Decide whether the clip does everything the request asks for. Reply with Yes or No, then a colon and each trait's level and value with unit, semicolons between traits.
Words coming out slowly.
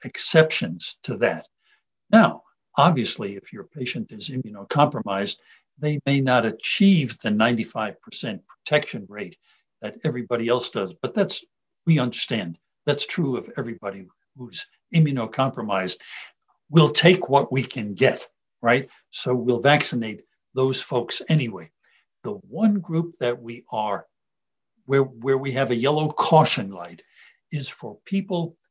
Yes: slow, 130 wpm